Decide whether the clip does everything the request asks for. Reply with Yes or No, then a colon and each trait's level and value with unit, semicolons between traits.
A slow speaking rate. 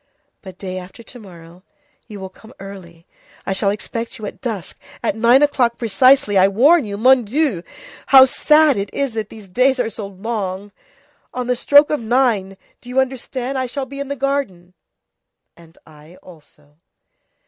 No: average, 175 wpm